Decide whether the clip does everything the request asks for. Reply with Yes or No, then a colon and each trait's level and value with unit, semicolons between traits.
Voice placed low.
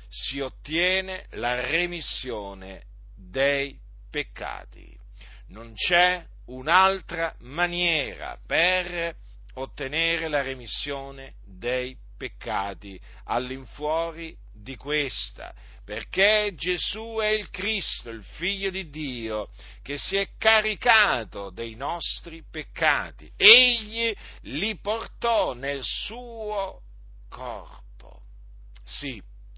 No: medium, 150 Hz